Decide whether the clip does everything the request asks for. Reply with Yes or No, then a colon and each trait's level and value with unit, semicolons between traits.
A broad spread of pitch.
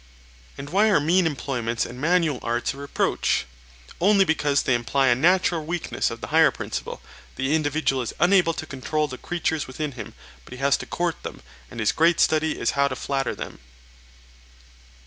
No: average, 4.2 semitones